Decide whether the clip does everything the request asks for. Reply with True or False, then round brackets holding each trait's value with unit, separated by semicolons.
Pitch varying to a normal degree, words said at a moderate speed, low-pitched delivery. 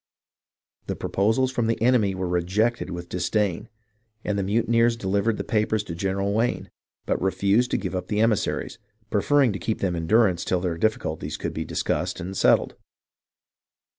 True (3.6 semitones; 170 wpm; 100 Hz)